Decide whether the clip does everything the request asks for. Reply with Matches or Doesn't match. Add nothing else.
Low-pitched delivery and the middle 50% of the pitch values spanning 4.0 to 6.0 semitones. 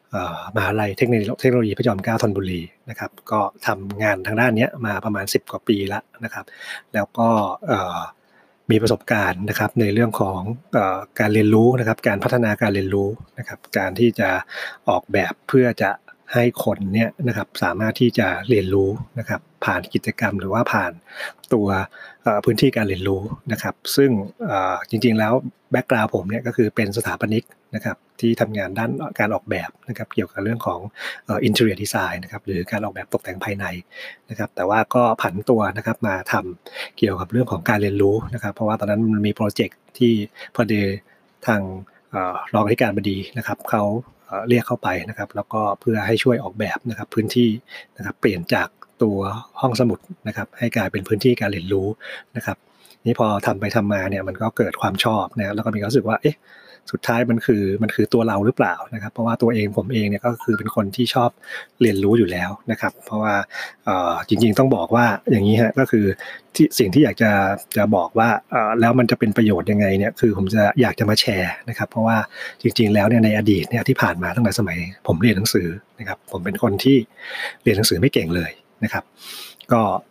Doesn't match